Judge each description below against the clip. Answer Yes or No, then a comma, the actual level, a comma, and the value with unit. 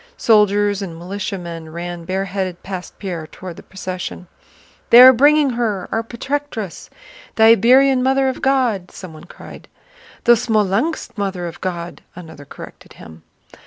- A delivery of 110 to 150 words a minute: Yes, slow, 135 wpm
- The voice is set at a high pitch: Yes, high, 195 Hz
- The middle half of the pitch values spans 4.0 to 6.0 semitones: Yes, average, 5.2 semitones